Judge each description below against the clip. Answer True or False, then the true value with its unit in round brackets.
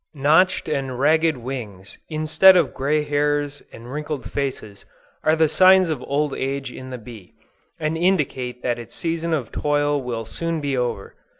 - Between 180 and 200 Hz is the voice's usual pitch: False (145 Hz)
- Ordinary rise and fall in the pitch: True (3.9 semitones)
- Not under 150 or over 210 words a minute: True (165 wpm)